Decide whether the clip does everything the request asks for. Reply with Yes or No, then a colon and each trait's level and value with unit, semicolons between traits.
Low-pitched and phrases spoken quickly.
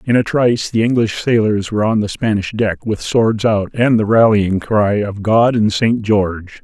Yes: low, 110 Hz; fast, 210 wpm